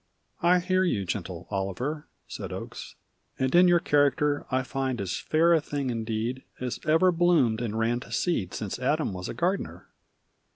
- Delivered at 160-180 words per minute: Yes, average, 170 wpm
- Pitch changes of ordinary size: No, wide, 6.7 semitones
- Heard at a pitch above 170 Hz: No, low, 135 Hz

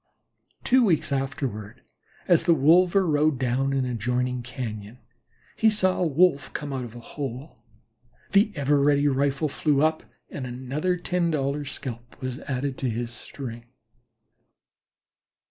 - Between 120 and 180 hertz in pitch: Yes, medium, 140 Hz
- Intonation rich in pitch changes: No, average, 3.8 semitones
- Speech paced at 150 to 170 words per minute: No, average, 140 wpm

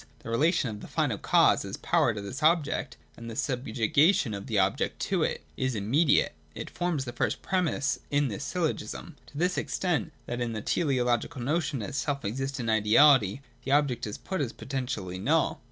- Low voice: Yes, low, 130 Hz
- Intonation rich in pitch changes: No, average, 4.7 semitones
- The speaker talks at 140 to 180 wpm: No, average, 190 wpm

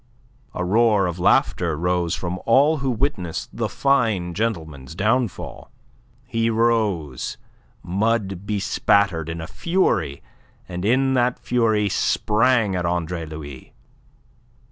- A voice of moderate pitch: No, low, 100 Hz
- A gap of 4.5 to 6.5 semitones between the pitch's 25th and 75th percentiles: Yes, average, 5.1 semitones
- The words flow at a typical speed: No, slow, 115 wpm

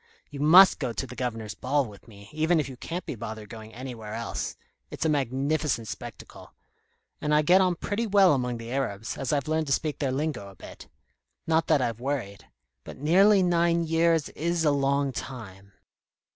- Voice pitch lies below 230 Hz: Yes, medium, 140 Hz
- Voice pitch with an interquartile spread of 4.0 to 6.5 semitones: Yes, wide, 5.6 semitones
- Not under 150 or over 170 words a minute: No, average, 190 wpm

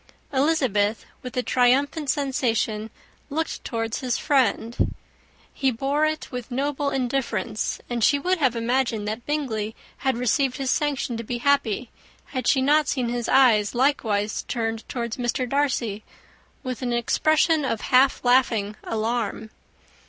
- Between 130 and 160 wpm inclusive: Yes, average, 140 wpm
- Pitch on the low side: No, very high, 250 Hz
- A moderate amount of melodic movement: Yes, average, 3.4 semitones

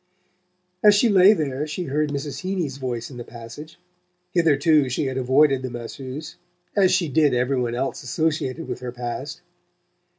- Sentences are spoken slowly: No, average, 165 wpm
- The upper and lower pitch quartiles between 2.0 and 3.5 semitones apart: No, average, 3.9 semitones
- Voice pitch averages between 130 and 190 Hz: Yes, medium, 140 Hz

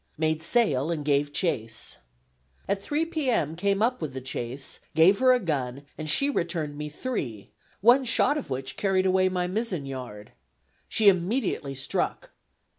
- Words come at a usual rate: Yes, average, 165 wpm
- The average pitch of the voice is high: No, medium, 170 Hz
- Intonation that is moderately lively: No, wide, 7.6 semitones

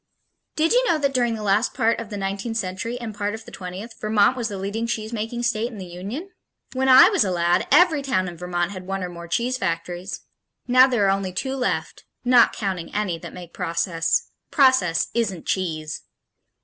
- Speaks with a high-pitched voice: Yes, high, 205 Hz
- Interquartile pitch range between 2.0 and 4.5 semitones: No, average, 4.9 semitones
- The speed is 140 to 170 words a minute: No, average, 200 wpm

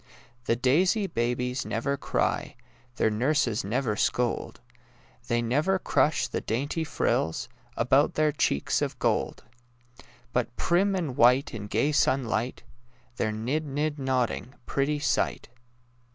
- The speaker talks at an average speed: No, slow, 125 wpm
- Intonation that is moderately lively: Yes, average, 4.2 semitones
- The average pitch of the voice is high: No, low, 130 Hz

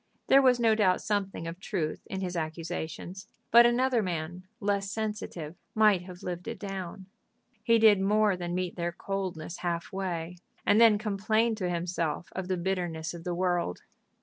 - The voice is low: No, medium, 185 Hz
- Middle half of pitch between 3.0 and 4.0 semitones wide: Yes, average, 3.4 semitones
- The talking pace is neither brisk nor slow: Yes, average, 170 wpm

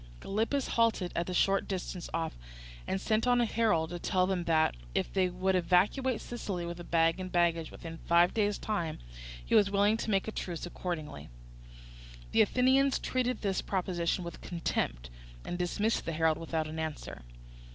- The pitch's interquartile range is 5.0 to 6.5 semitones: No, average, 3.9 semitones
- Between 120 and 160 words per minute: No, average, 170 wpm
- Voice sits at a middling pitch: Yes, medium, 180 Hz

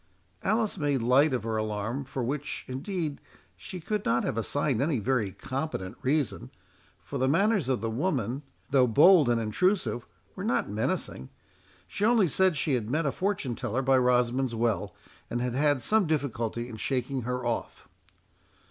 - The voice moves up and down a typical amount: Yes, average, 4.5 semitones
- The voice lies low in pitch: Yes, low, 130 Hz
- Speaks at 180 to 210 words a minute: No, average, 165 wpm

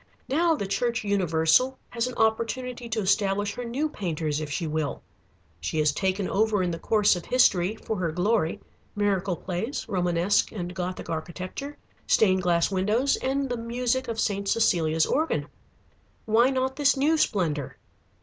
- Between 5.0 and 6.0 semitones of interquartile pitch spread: Yes, wide, 5.6 semitones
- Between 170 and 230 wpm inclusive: No, average, 160 wpm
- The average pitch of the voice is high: Yes, high, 205 Hz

